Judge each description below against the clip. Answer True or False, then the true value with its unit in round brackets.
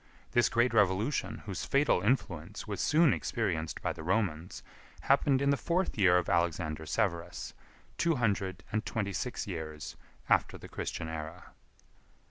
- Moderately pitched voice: False (95 Hz)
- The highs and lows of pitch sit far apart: True (6.3 semitones)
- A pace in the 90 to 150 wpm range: True (145 wpm)